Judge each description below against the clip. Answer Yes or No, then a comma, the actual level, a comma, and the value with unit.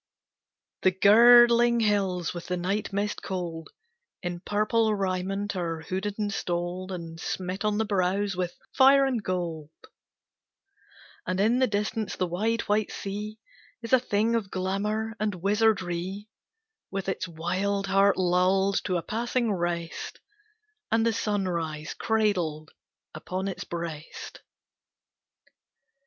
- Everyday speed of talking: No, slow, 125 wpm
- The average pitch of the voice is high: Yes, high, 195 Hz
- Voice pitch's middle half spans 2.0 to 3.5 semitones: Yes, average, 3.0 semitones